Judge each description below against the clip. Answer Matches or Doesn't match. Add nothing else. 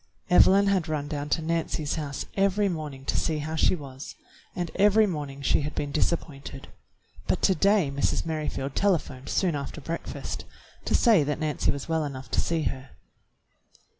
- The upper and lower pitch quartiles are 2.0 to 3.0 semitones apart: Doesn't match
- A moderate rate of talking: Matches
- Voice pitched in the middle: Matches